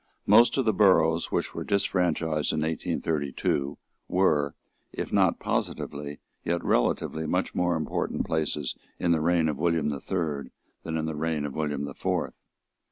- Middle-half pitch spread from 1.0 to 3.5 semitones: Yes, average, 2.7 semitones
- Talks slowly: No, average, 160 wpm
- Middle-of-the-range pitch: No, very low, 80 Hz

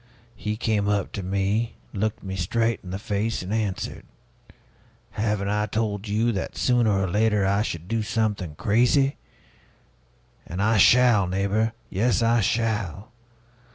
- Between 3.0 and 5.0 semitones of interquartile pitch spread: No, narrow, 2.5 semitones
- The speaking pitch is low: Yes, low, 105 Hz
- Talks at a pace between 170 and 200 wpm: No, average, 145 wpm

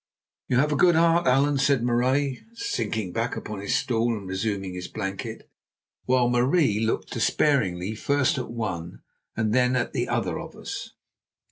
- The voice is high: No, low, 120 Hz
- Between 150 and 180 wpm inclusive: Yes, average, 160 wpm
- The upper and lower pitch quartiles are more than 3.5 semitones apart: Yes, average, 4.5 semitones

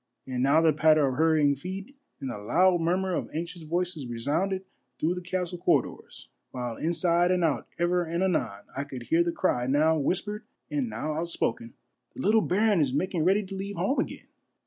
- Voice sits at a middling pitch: Yes, medium, 170 Hz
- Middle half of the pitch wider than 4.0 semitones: Yes, average, 4.4 semitones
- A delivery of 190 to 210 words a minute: Yes, average, 195 wpm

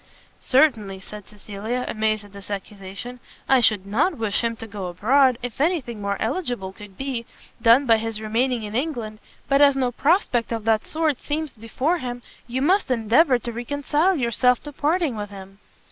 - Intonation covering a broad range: No, average, 4.5 semitones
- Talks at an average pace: Yes, average, 180 wpm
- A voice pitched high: Yes, high, 235 Hz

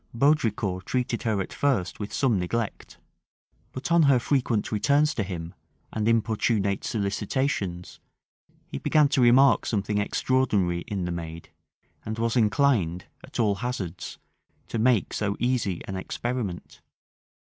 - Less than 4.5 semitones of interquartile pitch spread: No, average, 4.8 semitones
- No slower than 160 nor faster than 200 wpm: No, slow, 135 wpm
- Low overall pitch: Yes, low, 110 Hz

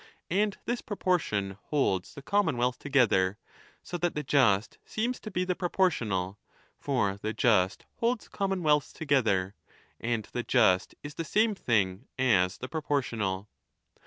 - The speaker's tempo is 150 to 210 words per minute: No, average, 140 wpm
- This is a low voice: Yes, low, 130 Hz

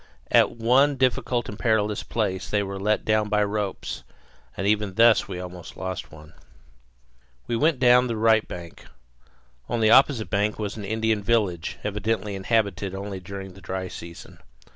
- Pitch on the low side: Yes, low, 105 Hz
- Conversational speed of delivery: Yes, average, 165 wpm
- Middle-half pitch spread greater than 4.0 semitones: No, average, 2.7 semitones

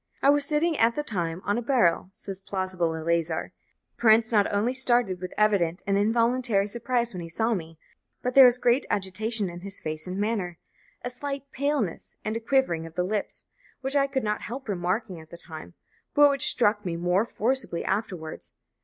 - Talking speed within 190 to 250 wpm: Yes, average, 195 wpm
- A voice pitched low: No, high, 210 Hz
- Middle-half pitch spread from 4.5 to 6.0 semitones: Yes, wide, 5.5 semitones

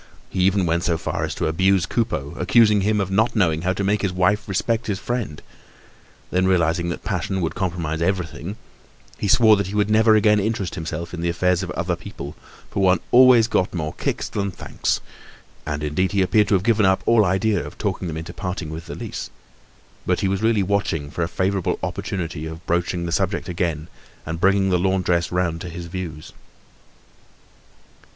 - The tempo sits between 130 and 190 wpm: No, average, 200 wpm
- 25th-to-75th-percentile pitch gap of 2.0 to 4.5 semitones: Yes, average, 3.0 semitones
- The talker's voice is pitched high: No, very low, 95 Hz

